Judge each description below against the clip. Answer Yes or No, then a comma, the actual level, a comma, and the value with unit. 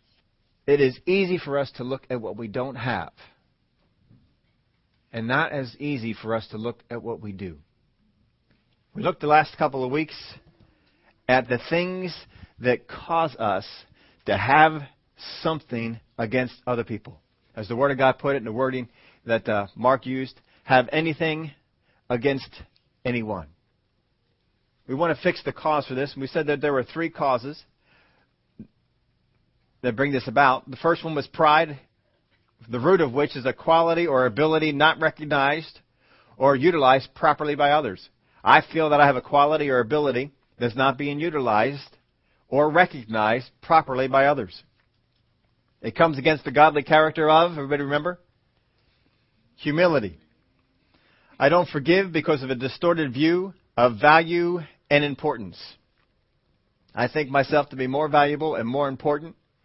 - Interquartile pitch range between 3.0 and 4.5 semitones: Yes, average, 4.0 semitones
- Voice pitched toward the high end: No, medium, 140 Hz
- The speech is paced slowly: No, average, 155 wpm